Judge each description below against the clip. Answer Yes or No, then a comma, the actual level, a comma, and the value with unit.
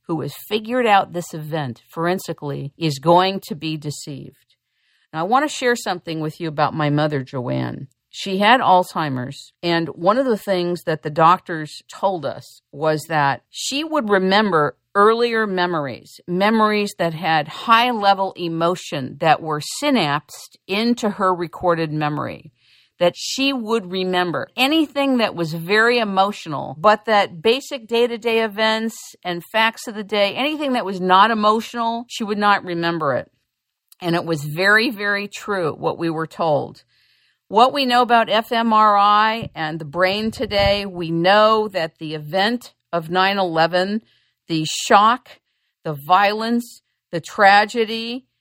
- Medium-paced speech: Yes, average, 150 wpm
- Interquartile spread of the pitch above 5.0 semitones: Yes, wide, 5.5 semitones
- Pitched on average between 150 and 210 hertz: Yes, high, 190 Hz